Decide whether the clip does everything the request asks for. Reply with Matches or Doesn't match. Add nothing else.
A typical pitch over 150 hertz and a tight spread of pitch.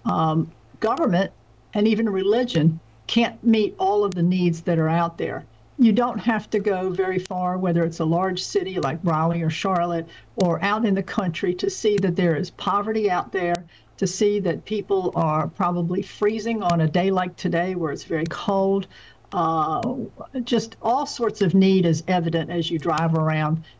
Doesn't match